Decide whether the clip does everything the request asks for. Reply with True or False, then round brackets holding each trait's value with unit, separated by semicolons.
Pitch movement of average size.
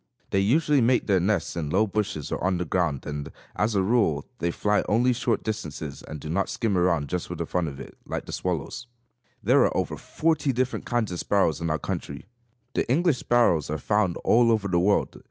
False (5.9 semitones)